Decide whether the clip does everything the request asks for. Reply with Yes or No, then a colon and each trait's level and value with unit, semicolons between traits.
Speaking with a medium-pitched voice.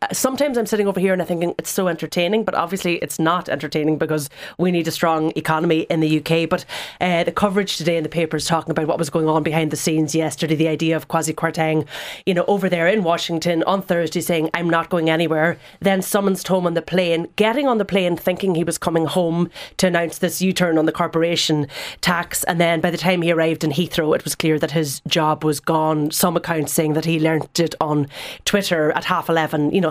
Yes: medium, 165 Hz